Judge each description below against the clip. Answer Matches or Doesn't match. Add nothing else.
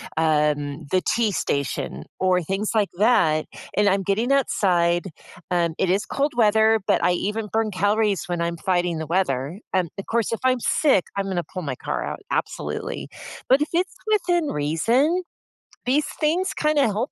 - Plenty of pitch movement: Matches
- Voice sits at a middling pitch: Doesn't match